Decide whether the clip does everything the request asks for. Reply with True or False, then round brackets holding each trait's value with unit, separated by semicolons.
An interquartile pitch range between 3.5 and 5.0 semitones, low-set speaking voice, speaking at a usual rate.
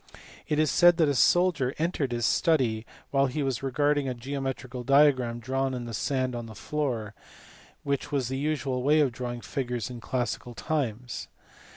False (3.1 semitones; 130 Hz; 170 wpm)